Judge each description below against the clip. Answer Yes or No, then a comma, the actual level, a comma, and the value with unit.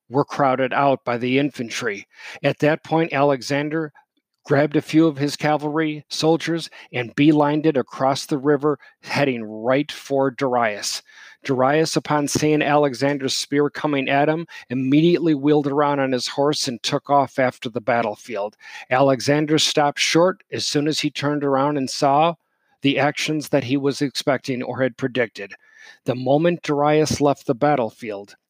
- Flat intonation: Yes, narrow, 2.1 semitones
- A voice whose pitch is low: No, medium, 145 Hz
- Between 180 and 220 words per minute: No, average, 155 wpm